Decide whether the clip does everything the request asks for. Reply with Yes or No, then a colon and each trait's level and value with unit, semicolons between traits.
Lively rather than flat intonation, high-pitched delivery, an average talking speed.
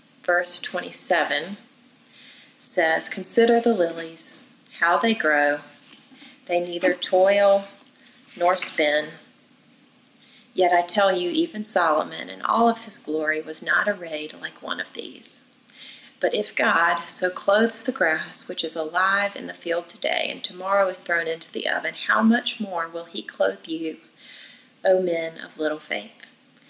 Yes: wide, 6.9 semitones; high, 195 Hz; average, 145 wpm